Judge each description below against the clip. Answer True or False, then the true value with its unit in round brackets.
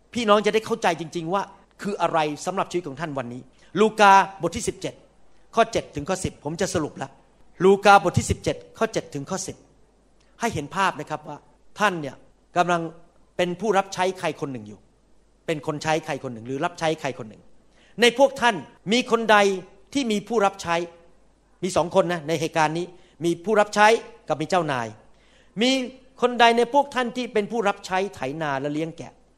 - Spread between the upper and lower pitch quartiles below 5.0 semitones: False (5.3 semitones)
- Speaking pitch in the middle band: True (180 Hz)